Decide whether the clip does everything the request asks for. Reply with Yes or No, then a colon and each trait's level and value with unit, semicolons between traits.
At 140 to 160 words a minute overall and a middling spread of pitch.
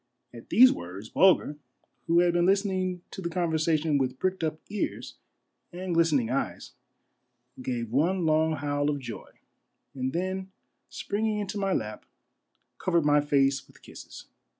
Yes: average, 150 wpm; average, 4.9 semitones